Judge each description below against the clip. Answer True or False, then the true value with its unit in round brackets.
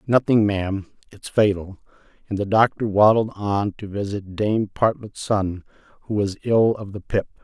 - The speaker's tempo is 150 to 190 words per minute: True (160 wpm)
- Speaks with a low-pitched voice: True (105 Hz)